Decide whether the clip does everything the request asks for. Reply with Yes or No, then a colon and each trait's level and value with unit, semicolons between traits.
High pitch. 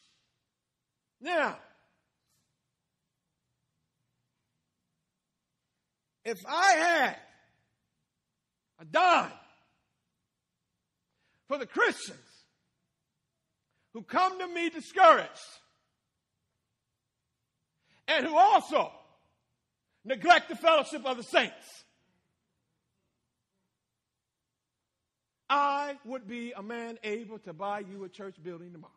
Yes: high, 240 Hz